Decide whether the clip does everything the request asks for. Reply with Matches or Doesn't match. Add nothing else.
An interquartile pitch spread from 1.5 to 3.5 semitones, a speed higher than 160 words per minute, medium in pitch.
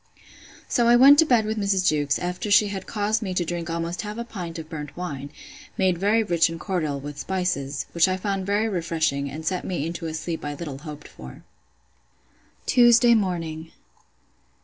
Doesn't match